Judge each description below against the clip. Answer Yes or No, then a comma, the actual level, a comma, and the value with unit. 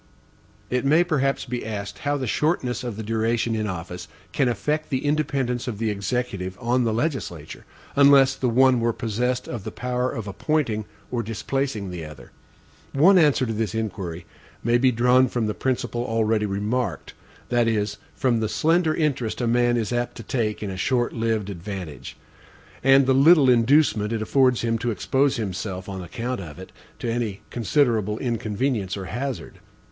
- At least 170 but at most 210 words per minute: Yes, average, 175 wpm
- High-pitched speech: No, low, 120 Hz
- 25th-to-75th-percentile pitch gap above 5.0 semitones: No, average, 3.7 semitones